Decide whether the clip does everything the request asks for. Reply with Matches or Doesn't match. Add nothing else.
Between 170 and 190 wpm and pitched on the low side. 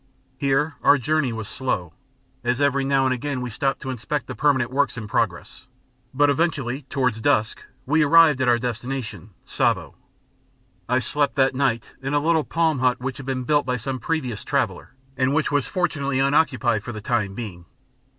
Matches